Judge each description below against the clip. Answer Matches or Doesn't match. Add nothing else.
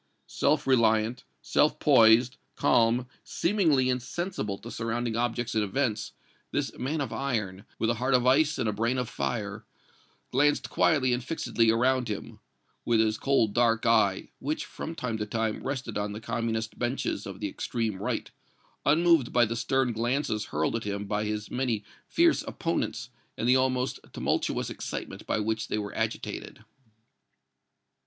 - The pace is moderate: Matches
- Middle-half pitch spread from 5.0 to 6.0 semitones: Doesn't match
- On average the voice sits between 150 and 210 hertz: Doesn't match